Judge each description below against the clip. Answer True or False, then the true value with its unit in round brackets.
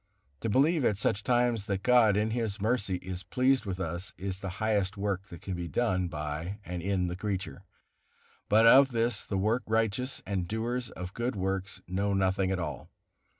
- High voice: False (100 Hz)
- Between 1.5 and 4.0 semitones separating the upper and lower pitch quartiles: True (3.5 semitones)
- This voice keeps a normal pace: True (190 wpm)